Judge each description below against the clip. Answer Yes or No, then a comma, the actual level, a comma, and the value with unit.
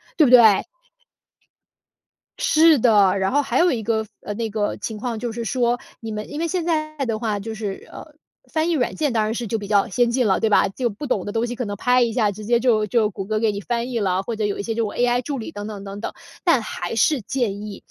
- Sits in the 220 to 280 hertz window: Yes, high, 225 Hz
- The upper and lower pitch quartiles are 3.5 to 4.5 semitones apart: No, average, 3.1 semitones